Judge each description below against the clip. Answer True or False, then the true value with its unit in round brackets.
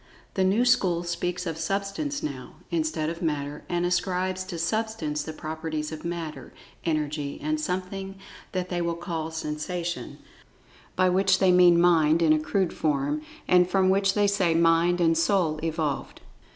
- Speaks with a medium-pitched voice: True (170 Hz)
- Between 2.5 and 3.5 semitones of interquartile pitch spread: True (3.0 semitones)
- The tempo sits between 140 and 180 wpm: True (160 wpm)